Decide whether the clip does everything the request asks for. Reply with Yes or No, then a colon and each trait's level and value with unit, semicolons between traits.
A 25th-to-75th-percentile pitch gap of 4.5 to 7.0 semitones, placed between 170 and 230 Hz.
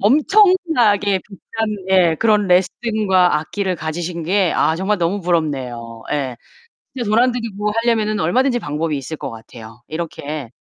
Yes: average, 5.3 semitones; high, 190 Hz